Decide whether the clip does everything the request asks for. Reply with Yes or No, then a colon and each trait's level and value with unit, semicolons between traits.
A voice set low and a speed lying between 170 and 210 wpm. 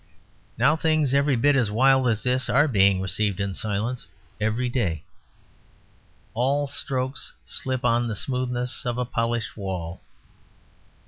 No: low, 120 Hz; slow, 135 wpm